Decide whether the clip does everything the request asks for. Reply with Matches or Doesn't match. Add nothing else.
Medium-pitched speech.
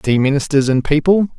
Matches